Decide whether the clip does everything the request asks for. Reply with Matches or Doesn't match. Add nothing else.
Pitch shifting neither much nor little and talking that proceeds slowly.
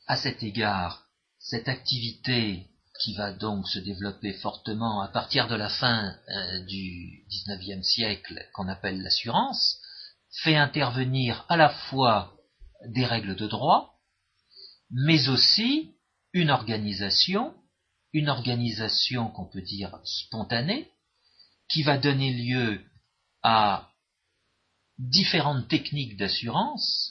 Doesn't match